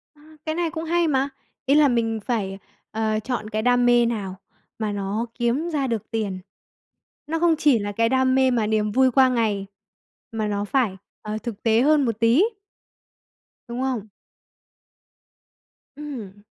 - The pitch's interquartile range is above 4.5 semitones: No, average, 3.8 semitones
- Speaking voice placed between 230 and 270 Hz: Yes, high, 235 Hz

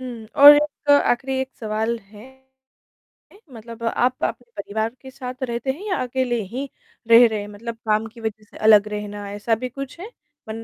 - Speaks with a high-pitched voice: Yes, high, 235 Hz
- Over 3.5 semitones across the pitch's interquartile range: No, average, 3.1 semitones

